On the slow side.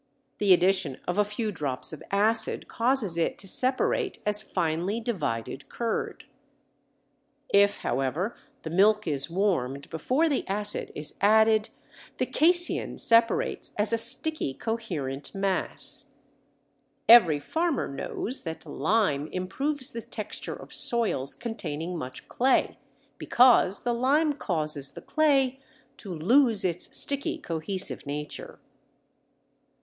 Yes: slow, 120 wpm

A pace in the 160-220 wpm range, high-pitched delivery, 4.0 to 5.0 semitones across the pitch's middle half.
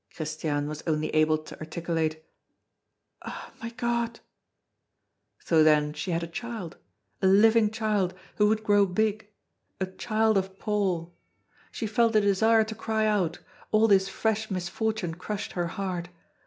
No: average, 145 wpm; high, 195 Hz; average, 4.6 semitones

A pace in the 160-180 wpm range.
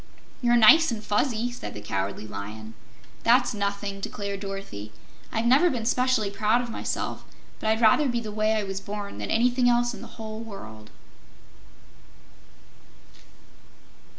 No: average, 150 wpm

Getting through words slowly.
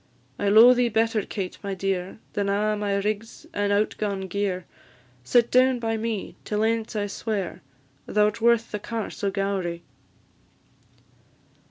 No: average, 155 wpm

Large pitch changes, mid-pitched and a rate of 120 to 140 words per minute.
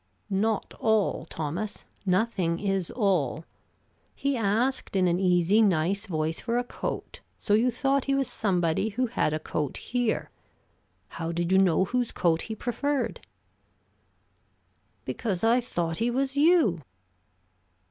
No: wide, 5.8 semitones; high, 200 Hz; slow, 135 wpm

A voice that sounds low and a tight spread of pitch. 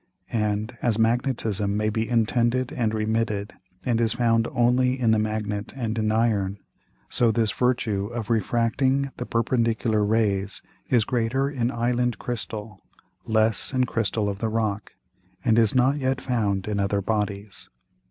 Yes: low, 115 Hz; narrow, 2.3 semitones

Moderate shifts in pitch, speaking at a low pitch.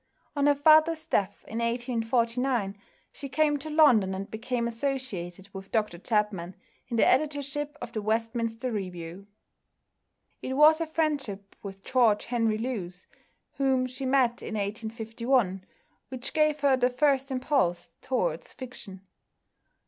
No: average, 4.7 semitones; high, 240 Hz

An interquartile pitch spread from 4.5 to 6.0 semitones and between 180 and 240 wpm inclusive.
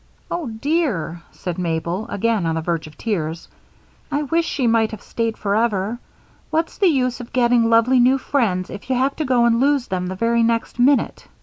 Yes: wide, 5.4 semitones; average, 195 wpm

